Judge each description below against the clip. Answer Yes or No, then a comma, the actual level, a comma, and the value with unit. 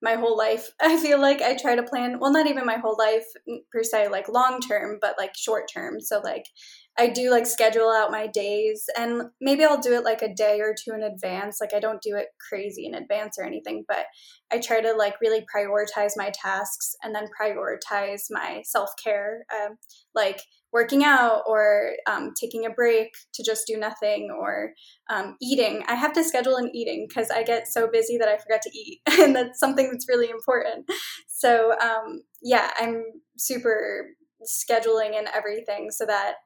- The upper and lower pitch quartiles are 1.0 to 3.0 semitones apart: Yes, average, 2.7 semitones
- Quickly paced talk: No, average, 195 wpm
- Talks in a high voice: Yes, high, 225 Hz